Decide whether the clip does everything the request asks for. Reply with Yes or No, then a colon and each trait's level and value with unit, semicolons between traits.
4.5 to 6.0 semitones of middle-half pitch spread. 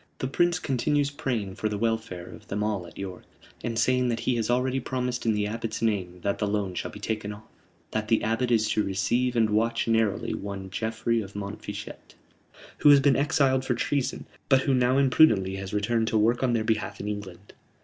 No: average, 3.6 semitones